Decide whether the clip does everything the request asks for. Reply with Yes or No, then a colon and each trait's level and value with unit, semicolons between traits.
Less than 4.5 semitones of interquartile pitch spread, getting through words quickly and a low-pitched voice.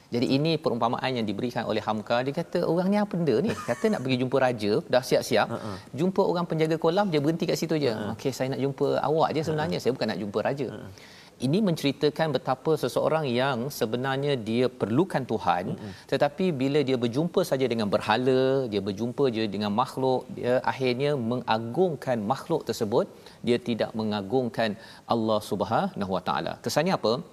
No: average, 4.9 semitones; fast, 165 wpm; low, 130 Hz